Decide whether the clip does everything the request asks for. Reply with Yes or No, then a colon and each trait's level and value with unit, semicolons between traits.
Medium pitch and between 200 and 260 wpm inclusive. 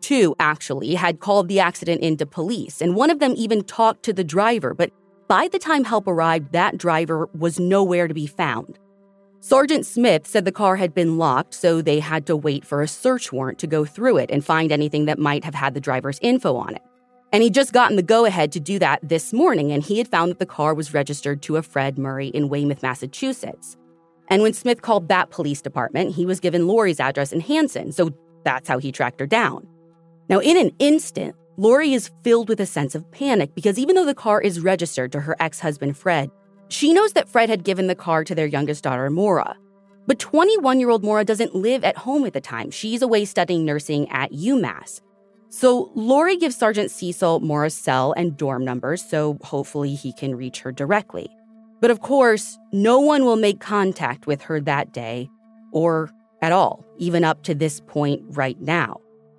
Yes: medium, 175 Hz; fast, 205 wpm